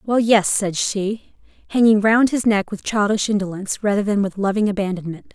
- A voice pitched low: No, high, 205 Hz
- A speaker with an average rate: Yes, average, 180 wpm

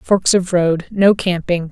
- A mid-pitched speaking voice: Yes, medium, 180 Hz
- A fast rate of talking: No, average, 140 wpm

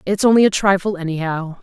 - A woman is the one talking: Yes, female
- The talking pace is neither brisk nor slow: Yes, average, 185 wpm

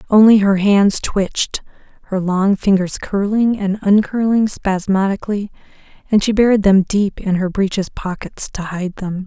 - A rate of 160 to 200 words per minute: No, average, 150 wpm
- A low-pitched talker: No, high, 200 Hz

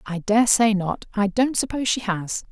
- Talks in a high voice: Yes, high, 215 Hz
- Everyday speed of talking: Yes, average, 190 wpm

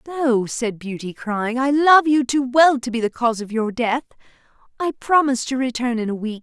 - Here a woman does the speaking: Yes, female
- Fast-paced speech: Yes, fast, 215 wpm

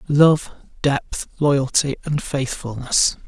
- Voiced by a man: Yes, male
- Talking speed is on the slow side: Yes, slow, 90 wpm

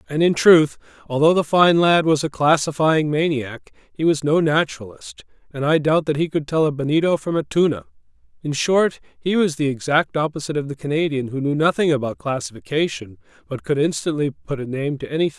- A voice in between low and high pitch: Yes, medium, 150 Hz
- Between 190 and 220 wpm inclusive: Yes, average, 200 wpm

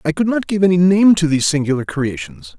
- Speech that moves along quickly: Yes, fast, 230 wpm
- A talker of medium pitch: Yes, medium, 175 Hz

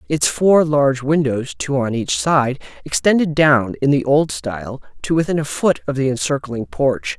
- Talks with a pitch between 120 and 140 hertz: Yes, low, 135 Hz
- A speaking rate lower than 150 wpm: No, average, 185 wpm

